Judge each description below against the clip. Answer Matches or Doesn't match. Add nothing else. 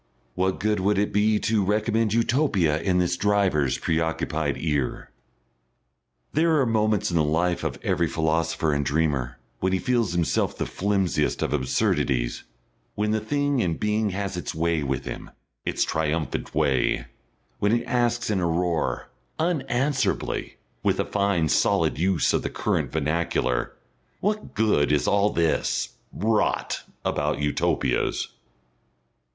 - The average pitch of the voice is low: Matches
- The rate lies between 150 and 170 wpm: Doesn't match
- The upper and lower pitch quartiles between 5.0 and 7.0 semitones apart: Matches